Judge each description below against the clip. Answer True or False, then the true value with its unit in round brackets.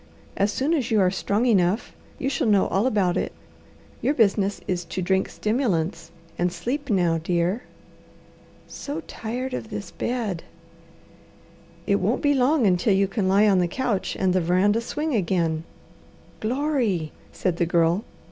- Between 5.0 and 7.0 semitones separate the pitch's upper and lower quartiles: True (5.3 semitones)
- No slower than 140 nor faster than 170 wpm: True (155 wpm)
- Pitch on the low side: False (200 Hz)